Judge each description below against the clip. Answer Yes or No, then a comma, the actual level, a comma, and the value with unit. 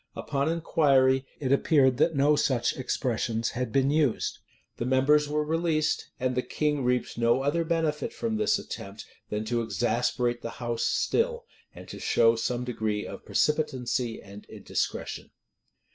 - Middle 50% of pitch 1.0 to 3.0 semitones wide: No, average, 4.1 semitones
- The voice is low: Yes, low, 130 Hz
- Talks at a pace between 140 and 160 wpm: Yes, average, 150 wpm